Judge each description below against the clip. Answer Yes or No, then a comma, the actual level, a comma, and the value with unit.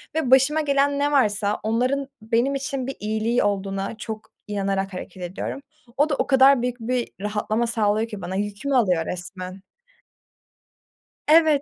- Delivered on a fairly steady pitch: No, average, 5.2 semitones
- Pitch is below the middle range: No, high, 230 Hz